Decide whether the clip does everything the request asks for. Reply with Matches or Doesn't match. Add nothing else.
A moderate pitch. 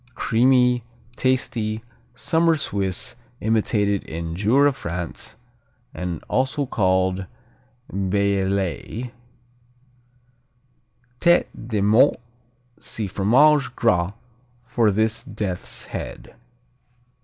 Doesn't match